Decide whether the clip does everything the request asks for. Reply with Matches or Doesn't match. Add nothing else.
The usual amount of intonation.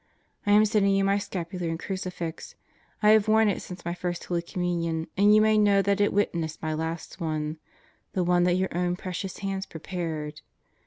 Matches